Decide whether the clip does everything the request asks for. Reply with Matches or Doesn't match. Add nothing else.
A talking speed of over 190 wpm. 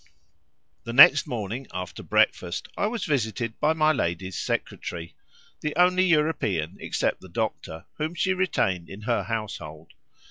Doesn't match